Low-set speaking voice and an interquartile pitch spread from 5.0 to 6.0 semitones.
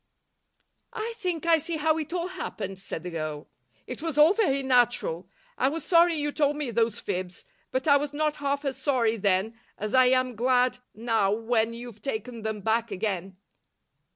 No: very high, 250 Hz; wide, 5.4 semitones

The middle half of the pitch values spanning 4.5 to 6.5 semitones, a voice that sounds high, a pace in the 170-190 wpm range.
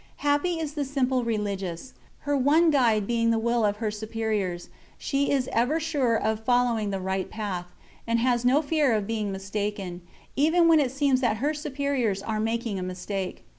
Yes: average, 5.1 semitones; high, 230 Hz; average, 180 wpm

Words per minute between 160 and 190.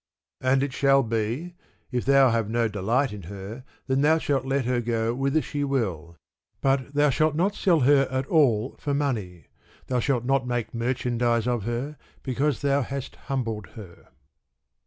Yes: average, 170 wpm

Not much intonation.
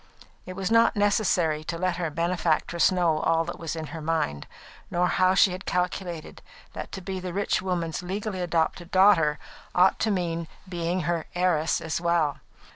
Yes: narrow, 2.1 semitones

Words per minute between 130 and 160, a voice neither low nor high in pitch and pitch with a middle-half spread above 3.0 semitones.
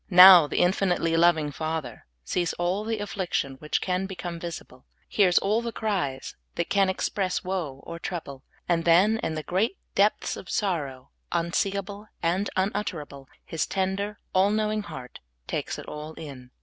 Yes: average, 155 wpm; medium, 180 Hz; average, 4.0 semitones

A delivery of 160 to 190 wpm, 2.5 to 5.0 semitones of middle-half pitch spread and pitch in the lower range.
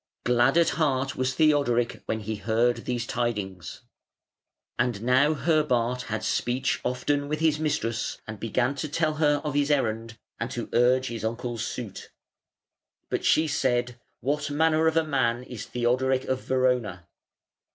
No: average, 150 wpm; average, 3.6 semitones; low, 125 Hz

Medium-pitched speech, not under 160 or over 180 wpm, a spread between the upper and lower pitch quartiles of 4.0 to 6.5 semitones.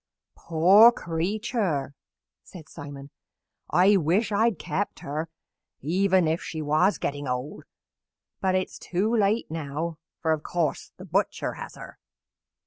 No: medium, 170 Hz; slow, 135 wpm; average, 4.6 semitones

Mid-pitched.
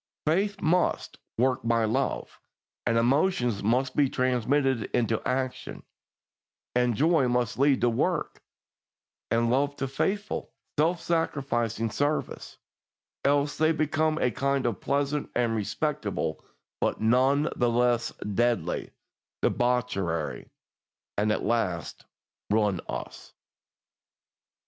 No: low, 125 Hz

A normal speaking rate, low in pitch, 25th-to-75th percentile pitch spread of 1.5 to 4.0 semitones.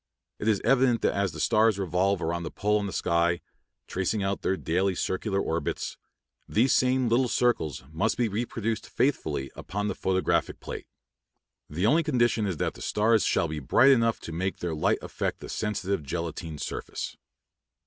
No: average, 175 wpm; low, 100 Hz; average, 5.0 semitones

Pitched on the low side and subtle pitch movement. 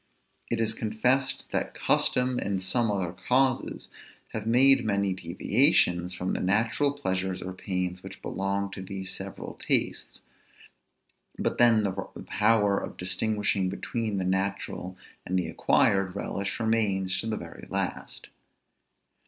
No: low, 100 Hz; average, 3.3 semitones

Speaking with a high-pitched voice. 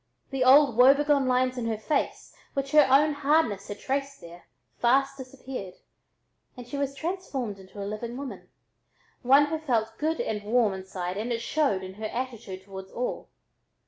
Yes: very high, 250 Hz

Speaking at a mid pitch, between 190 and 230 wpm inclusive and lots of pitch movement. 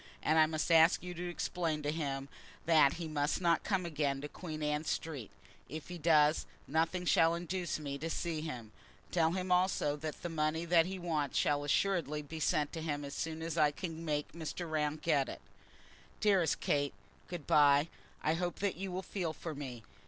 No: medium, 160 Hz; average, 195 wpm; narrow, 2.5 semitones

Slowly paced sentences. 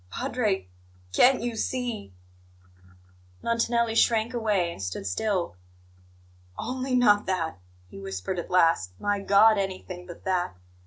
Yes: slow, 125 wpm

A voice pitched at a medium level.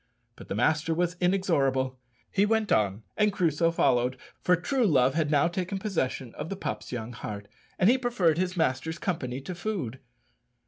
Yes: medium, 165 Hz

